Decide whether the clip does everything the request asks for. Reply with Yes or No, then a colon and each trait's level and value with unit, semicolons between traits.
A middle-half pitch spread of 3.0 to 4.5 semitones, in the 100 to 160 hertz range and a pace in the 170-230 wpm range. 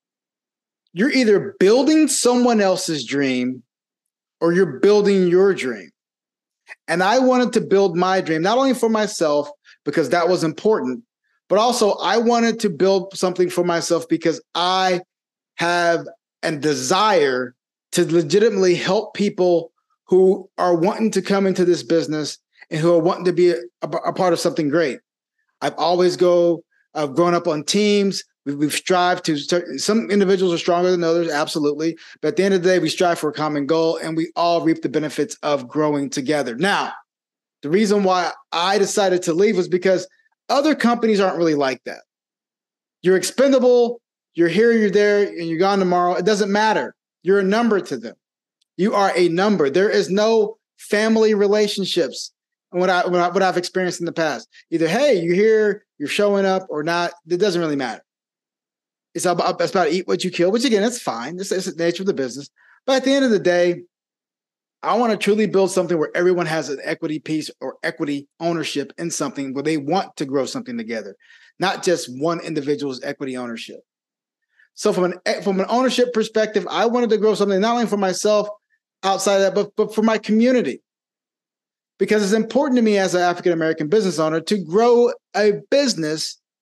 No: average, 4.0 semitones; medium, 185 Hz; average, 185 wpm